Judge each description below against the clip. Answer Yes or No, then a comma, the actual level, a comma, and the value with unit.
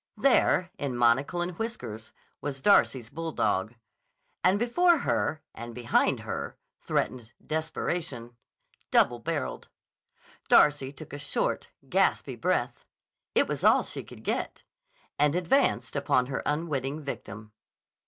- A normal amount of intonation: No, wide, 5.9 semitones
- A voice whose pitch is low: No, medium, 145 Hz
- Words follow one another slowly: Yes, slow, 115 wpm